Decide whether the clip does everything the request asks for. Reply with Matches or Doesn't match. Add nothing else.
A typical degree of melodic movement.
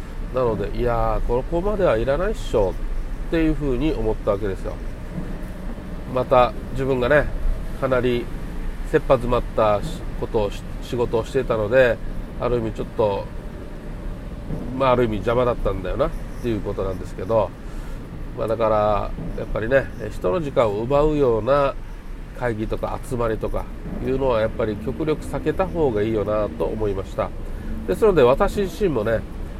Matches